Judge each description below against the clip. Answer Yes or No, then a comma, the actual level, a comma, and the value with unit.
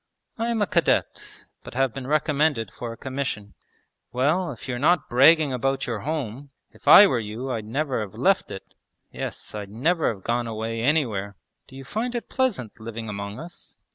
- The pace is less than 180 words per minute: No, average, 185 wpm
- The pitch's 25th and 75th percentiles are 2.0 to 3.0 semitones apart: No, wide, 5.6 semitones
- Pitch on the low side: Yes, low, 130 Hz